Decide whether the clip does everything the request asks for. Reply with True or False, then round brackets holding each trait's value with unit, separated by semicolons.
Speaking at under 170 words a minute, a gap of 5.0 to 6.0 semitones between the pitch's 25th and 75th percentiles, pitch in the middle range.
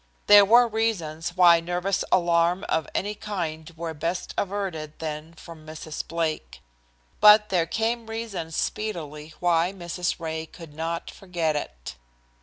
False (135 wpm; 3.7 semitones; 170 Hz)